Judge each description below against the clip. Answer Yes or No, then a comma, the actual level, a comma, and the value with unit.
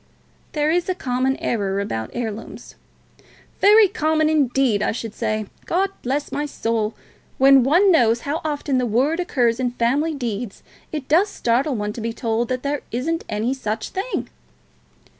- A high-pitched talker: Yes, very high, 255 Hz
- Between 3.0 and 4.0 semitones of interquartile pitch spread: No, average, 5.1 semitones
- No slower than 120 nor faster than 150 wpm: No, average, 160 wpm